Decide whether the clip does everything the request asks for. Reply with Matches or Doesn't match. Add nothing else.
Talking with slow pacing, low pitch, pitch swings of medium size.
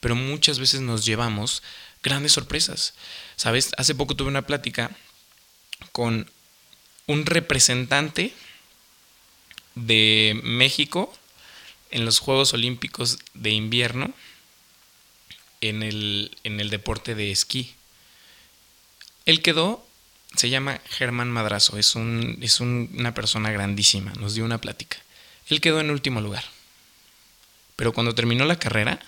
Matches